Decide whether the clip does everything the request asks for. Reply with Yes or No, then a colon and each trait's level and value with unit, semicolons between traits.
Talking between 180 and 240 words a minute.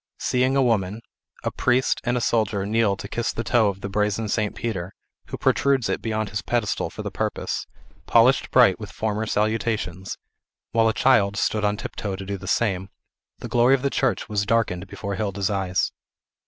Yes: average, 190 wpm